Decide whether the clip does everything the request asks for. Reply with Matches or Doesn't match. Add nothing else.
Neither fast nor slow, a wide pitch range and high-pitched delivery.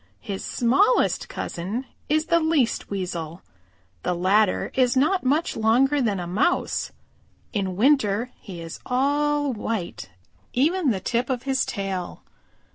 Doesn't match